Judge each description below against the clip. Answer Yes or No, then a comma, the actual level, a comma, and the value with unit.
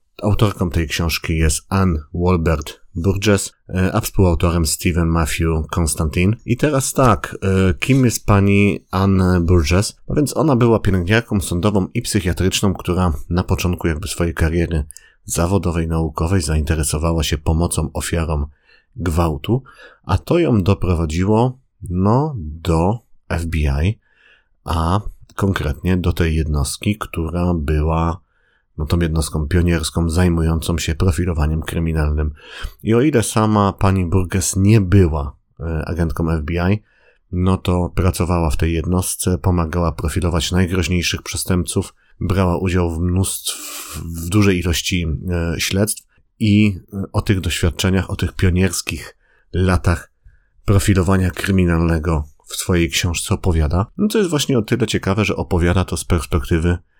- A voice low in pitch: Yes, very low, 90 Hz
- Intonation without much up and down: No, average, 3.0 semitones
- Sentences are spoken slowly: No, average, 125 wpm